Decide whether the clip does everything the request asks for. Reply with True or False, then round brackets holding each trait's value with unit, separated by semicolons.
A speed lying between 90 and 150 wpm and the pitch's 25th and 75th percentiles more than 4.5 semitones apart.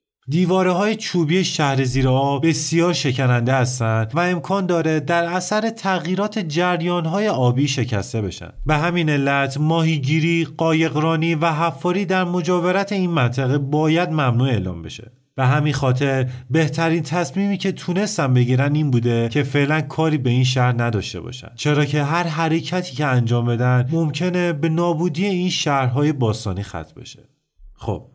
True (145 wpm; 5.1 semitones)